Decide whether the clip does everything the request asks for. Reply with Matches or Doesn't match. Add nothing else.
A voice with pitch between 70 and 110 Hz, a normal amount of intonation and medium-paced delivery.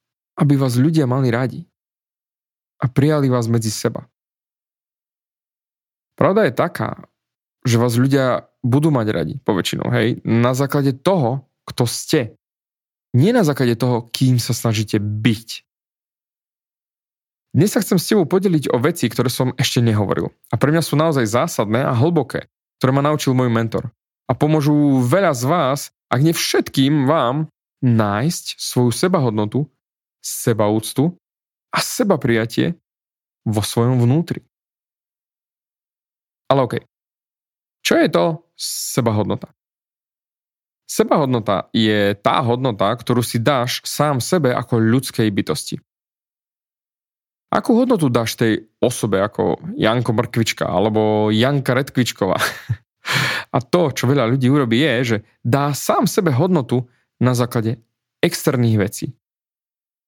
Doesn't match